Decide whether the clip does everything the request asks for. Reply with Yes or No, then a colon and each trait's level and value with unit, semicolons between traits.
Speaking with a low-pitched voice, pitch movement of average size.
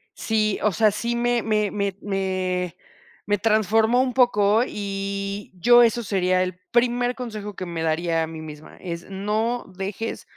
No: high, 205 Hz; average, 3.5 semitones